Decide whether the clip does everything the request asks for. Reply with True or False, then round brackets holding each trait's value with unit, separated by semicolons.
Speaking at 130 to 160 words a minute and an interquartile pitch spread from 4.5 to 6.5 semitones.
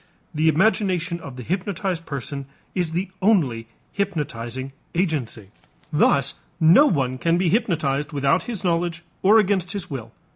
True (140 wpm; 5.2 semitones)